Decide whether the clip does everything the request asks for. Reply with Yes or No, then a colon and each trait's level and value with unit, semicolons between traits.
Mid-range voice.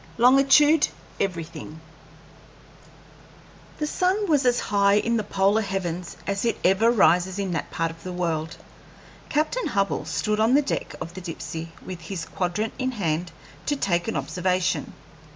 No: high, 195 Hz